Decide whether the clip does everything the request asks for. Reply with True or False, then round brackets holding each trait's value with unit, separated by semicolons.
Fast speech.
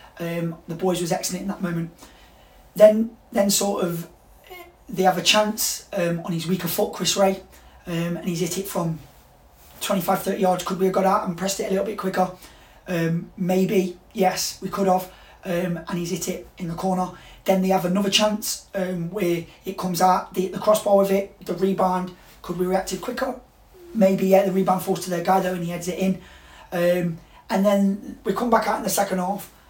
True (210 wpm)